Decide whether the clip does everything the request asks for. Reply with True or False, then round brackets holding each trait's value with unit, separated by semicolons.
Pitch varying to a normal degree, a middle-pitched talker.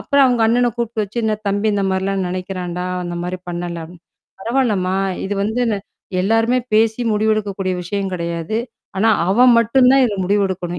False (3.7 semitones; 205 Hz)